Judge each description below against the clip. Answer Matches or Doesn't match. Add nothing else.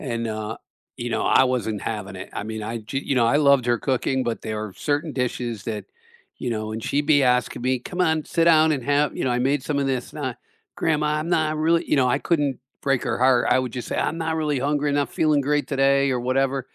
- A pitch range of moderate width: Matches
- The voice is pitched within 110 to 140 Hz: Matches